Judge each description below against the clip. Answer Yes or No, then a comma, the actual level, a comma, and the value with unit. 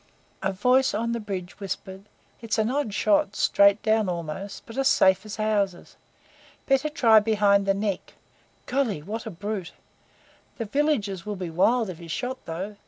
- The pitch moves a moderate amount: Yes, average, 3.0 semitones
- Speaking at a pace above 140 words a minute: Yes, average, 170 wpm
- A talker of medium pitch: No, high, 210 Hz